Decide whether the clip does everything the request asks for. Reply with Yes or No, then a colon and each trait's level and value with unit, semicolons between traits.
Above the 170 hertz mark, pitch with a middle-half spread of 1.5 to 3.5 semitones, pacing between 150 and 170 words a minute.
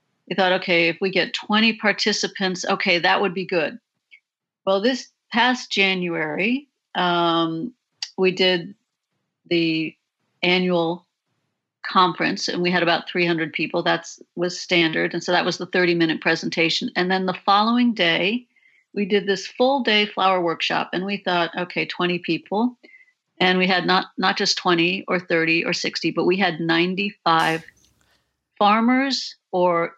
Yes: medium, 185 Hz; average, 2.9 semitones; average, 155 wpm